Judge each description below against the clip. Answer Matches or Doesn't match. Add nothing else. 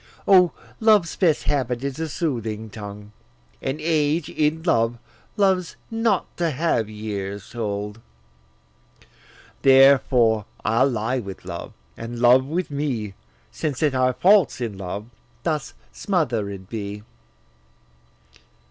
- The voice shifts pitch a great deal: Matches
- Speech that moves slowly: Matches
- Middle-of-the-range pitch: Doesn't match